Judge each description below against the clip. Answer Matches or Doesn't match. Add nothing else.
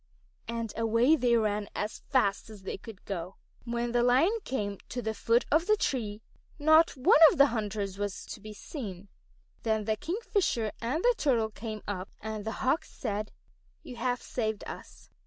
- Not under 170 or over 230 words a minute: Matches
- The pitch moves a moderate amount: Matches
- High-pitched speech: Matches